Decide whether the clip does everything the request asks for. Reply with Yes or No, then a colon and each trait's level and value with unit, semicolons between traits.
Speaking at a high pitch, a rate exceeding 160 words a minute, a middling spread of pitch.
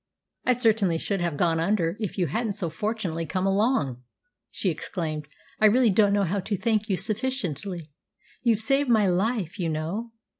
Yes: high, 200 Hz; average, 180 wpm; average, 4.6 semitones